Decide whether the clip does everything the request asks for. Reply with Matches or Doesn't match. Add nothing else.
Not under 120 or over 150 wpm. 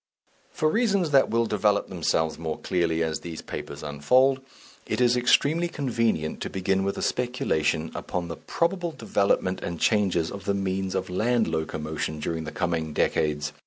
Doesn't match